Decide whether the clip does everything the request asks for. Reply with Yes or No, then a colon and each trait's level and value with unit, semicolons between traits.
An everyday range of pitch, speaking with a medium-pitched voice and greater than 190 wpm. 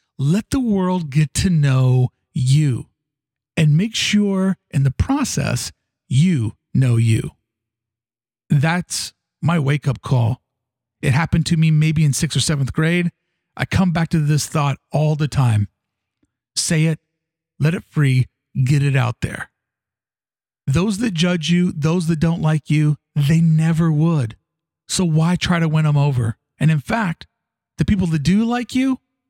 No: average, 4.2 semitones; medium, 155 Hz; average, 160 wpm